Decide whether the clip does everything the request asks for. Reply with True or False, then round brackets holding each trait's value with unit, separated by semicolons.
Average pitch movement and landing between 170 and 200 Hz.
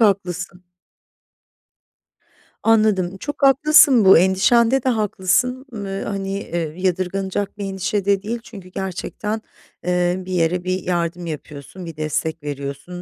True (3.0 semitones; 190 Hz)